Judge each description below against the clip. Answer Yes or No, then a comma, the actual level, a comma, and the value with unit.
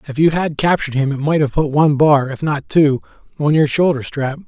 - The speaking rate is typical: No, fast, 240 wpm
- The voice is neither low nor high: Yes, medium, 145 Hz